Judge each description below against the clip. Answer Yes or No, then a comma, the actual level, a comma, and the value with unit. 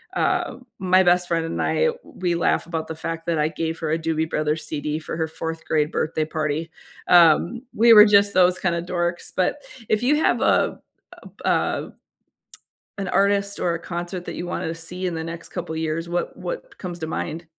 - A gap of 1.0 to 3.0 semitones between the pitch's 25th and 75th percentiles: Yes, narrow, 2.4 semitones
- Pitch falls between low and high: Yes, medium, 170 Hz